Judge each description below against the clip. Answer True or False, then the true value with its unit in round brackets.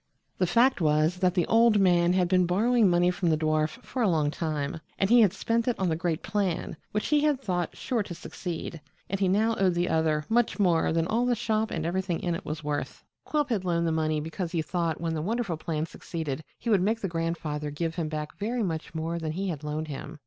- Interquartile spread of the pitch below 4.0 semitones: False (4.3 semitones)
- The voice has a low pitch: False (175 Hz)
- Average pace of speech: False (235 wpm)